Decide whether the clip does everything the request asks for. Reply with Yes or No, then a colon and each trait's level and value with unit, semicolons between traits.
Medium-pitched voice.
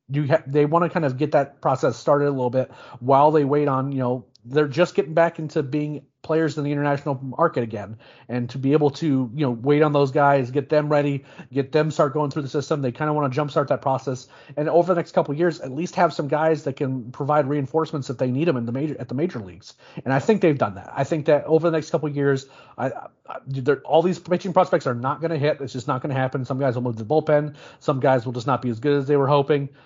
Yes: medium, 145 Hz